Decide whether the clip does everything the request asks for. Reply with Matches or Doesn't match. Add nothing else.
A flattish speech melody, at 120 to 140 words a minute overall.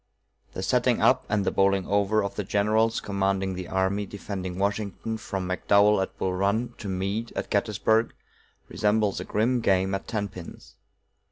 Doesn't match